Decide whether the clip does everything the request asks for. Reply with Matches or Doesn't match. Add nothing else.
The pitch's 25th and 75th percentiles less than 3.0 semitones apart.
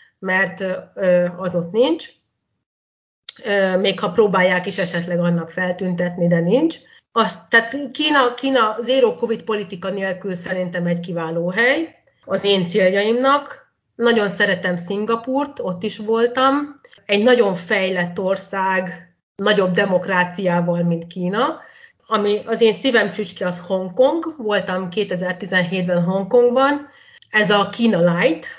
Doesn't match